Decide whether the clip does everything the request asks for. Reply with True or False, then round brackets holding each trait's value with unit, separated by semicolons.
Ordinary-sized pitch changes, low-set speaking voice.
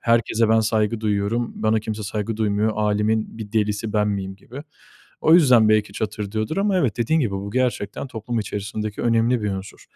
False (1.8 semitones; 110 Hz)